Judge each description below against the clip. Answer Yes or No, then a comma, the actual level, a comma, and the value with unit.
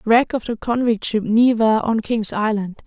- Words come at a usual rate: Yes, average, 190 wpm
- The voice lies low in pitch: No, high, 225 Hz